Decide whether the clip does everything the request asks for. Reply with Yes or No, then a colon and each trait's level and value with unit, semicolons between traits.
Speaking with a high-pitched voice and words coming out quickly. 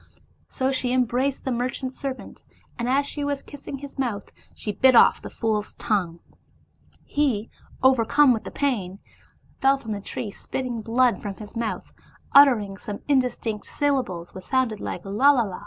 No: high, 245 Hz; average, 165 wpm